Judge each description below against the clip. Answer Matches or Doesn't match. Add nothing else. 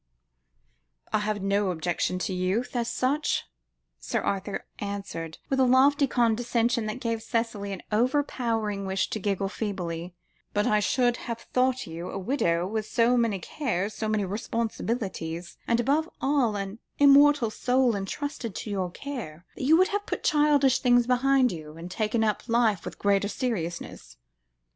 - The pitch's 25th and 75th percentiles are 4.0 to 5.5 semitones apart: Matches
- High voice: Matches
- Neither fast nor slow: Matches